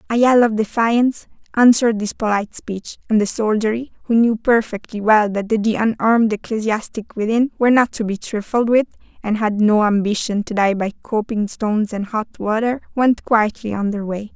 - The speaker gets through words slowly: No, average, 180 wpm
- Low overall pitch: No, high, 220 Hz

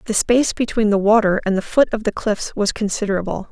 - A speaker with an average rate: No, fast, 220 wpm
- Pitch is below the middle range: No, high, 210 Hz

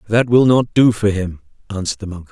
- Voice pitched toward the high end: No, low, 105 Hz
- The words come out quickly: Yes, fast, 235 wpm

